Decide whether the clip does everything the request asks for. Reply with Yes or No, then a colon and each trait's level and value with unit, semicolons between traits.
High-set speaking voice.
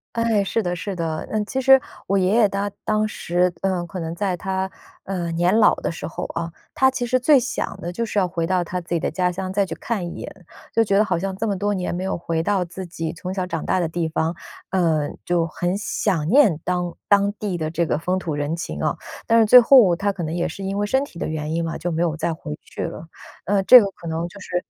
No: medium, 180 Hz